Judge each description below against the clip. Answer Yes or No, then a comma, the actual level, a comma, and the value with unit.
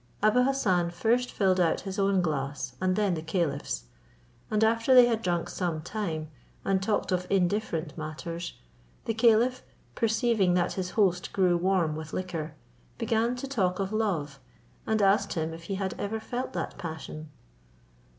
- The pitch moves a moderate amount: Yes, average, 4.7 semitones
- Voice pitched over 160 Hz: Yes, medium, 185 Hz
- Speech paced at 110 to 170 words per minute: Yes, average, 160 wpm